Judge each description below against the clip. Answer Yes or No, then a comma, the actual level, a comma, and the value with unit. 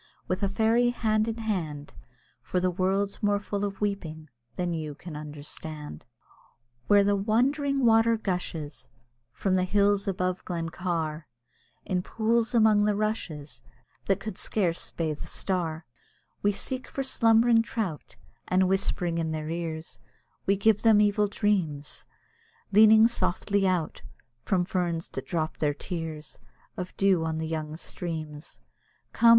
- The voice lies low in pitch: No, medium, 185 Hz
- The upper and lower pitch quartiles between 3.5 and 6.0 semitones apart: Yes, average, 4.7 semitones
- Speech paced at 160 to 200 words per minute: No, average, 145 wpm